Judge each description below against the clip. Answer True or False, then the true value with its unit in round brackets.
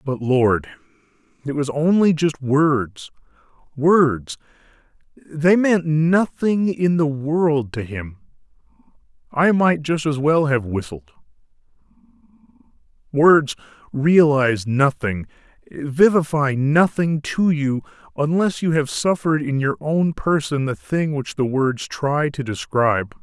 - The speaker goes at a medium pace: False (115 wpm)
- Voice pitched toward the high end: False (145 Hz)